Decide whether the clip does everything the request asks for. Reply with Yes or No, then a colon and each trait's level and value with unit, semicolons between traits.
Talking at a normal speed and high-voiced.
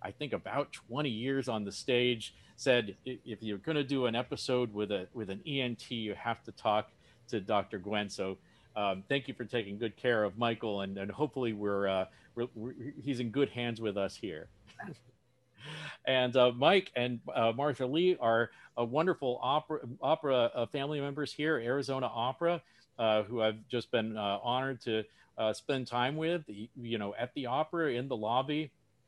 No: average, 185 wpm; low, 120 Hz